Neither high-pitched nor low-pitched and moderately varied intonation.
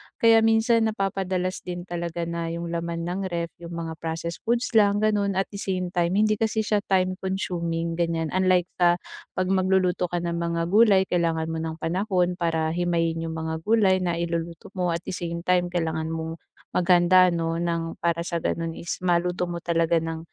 No: medium, 175 Hz; narrow, 2.0 semitones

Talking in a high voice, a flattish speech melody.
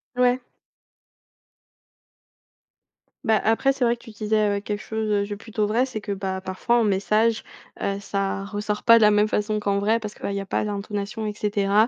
Yes: high, 210 Hz; narrow, 1.6 semitones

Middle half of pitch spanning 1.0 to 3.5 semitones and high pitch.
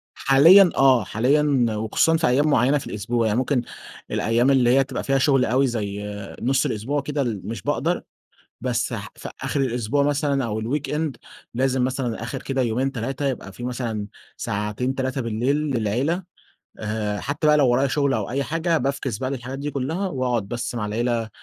No: average, 3.2 semitones; low, 130 Hz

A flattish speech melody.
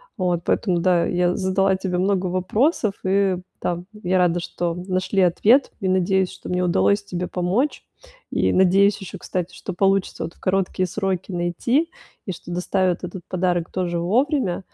Yes: narrow, 1.7 semitones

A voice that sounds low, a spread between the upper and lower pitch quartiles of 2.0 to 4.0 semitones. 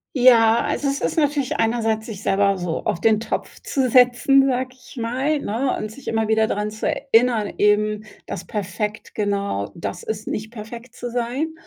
No: high, 225 Hz; average, 3.0 semitones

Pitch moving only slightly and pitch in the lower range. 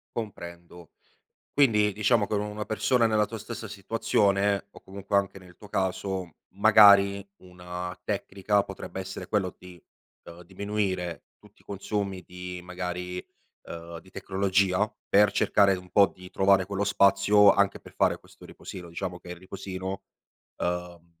Yes: narrow, 2.1 semitones; very low, 95 Hz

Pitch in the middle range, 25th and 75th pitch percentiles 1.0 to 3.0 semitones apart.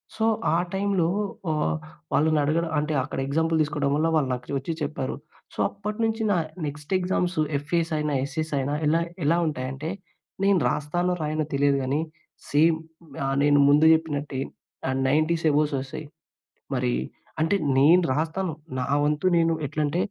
Yes: medium, 155 Hz; narrow, 2.6 semitones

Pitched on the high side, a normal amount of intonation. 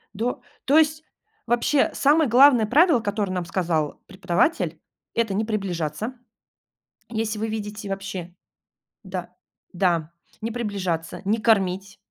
Yes: high, 210 Hz; average, 4.2 semitones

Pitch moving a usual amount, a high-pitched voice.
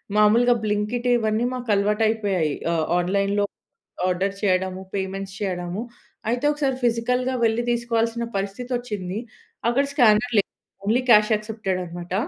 Yes: average, 3.6 semitones; high, 210 Hz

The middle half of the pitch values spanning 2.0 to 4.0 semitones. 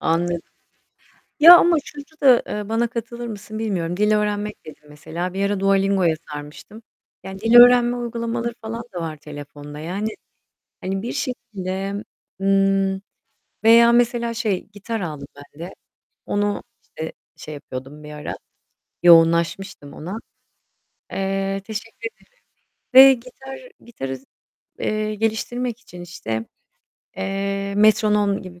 No: average, 4.9 semitones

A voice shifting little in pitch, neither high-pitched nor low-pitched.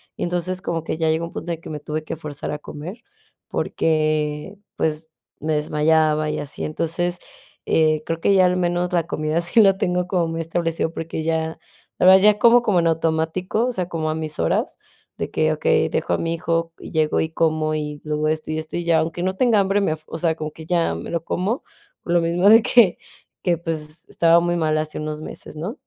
Yes: narrow, 2.2 semitones; medium, 165 Hz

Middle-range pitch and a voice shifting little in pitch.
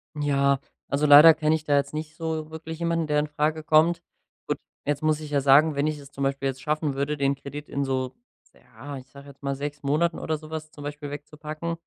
Yes: medium, 150 Hz; narrow, 1.8 semitones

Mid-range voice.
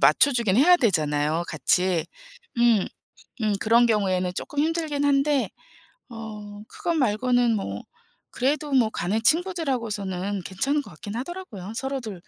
No: high, 225 Hz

